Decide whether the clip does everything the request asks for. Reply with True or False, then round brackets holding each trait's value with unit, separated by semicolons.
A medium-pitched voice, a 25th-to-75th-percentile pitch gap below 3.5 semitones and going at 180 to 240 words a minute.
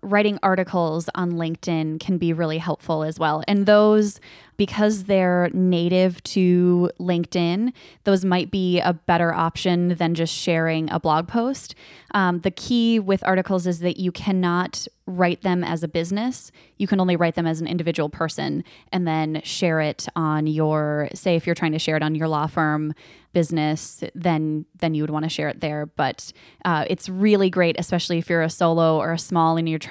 True (170 Hz; 2.6 semitones; 190 wpm)